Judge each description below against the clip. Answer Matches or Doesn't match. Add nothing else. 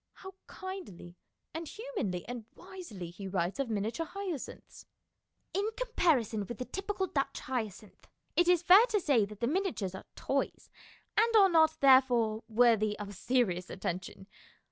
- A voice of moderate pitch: Doesn't match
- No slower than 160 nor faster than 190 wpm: Doesn't match